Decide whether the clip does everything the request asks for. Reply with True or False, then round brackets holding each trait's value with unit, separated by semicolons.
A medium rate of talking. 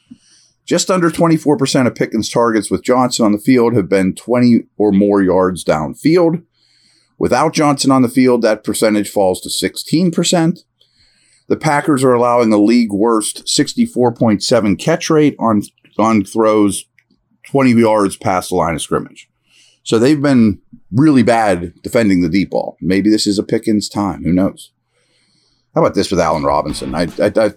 True (165 wpm)